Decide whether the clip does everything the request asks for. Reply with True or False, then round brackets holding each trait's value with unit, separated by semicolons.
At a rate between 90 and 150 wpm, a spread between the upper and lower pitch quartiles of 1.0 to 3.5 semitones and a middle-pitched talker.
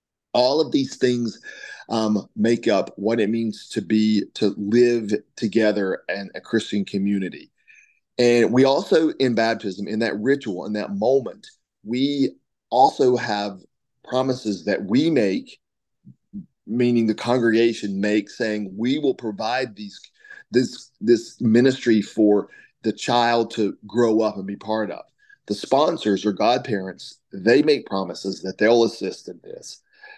False (140 wpm; 3.0 semitones; 115 Hz)